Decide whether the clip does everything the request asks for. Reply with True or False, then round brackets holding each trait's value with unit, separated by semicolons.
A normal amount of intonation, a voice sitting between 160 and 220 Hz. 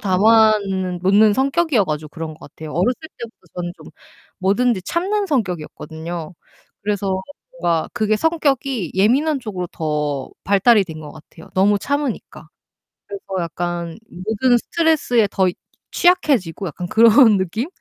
False (6.0 semitones; 200 Hz)